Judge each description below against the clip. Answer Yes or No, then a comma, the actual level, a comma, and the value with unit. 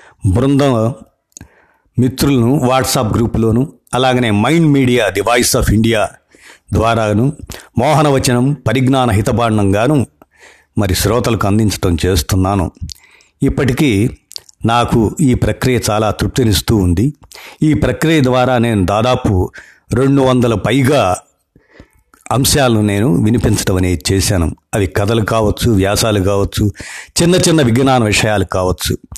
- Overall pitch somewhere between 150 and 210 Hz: No, low, 115 Hz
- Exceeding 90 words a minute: Yes, average, 100 wpm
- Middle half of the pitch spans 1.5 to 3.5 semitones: No, average, 4.3 semitones